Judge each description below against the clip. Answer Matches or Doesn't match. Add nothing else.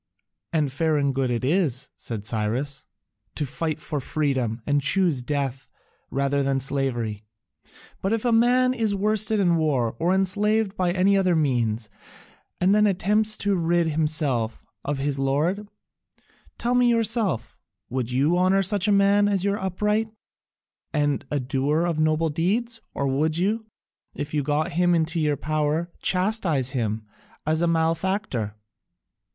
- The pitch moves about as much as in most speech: Doesn't match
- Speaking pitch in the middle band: Matches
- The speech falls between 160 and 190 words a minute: Doesn't match